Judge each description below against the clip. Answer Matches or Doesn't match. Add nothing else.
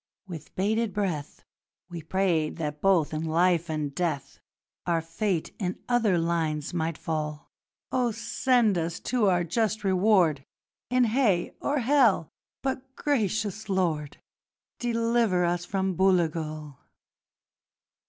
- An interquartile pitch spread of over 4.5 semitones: Matches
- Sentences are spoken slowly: Matches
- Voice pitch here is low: Doesn't match